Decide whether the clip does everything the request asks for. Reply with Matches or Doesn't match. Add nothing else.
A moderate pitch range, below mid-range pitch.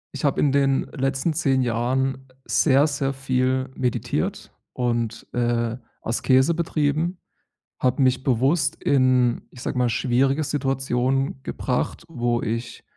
Doesn't match